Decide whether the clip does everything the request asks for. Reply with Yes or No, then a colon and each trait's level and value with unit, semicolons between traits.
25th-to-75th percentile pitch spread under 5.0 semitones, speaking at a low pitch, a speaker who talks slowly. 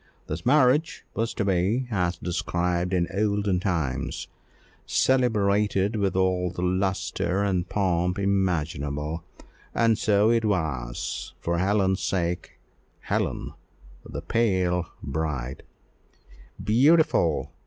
Yes: average, 3.2 semitones; very low, 95 Hz; slow, 100 wpm